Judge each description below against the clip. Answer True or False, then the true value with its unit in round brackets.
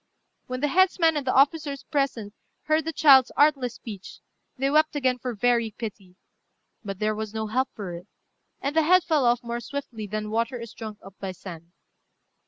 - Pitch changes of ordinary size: True (5.0 semitones)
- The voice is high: True (245 Hz)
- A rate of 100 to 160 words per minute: False (190 wpm)